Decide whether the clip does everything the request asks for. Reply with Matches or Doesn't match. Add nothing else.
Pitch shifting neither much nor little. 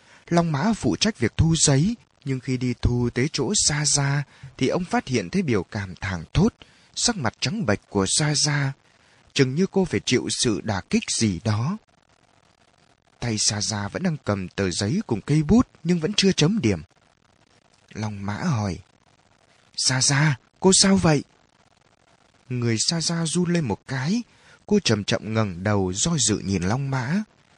Doesn't match